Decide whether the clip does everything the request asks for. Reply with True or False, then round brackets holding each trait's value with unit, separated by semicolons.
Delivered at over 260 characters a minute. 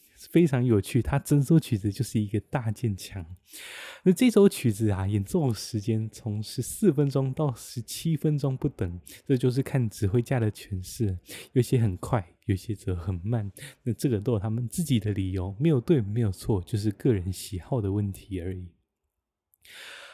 False (255 characters per minute)